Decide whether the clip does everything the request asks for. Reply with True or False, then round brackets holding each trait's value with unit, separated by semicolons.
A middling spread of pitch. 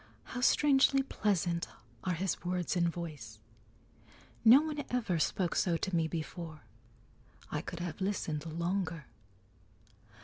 True (3.9 semitones)